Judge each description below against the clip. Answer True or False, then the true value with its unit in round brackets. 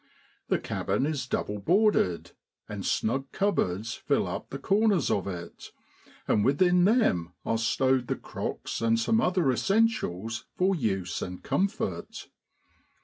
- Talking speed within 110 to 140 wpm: True (135 wpm)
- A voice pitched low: True (130 Hz)